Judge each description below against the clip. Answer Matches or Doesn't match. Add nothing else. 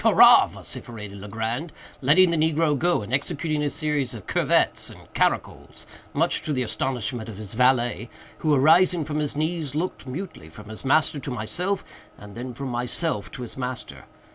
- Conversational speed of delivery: Matches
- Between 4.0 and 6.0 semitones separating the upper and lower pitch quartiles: Matches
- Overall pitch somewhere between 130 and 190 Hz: Matches